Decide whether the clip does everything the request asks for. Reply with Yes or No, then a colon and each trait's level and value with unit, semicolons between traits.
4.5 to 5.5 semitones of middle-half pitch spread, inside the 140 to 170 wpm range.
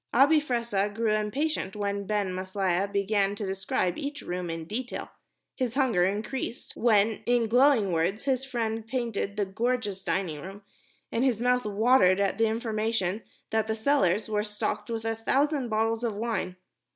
No: average, 3.3 semitones; average, 165 wpm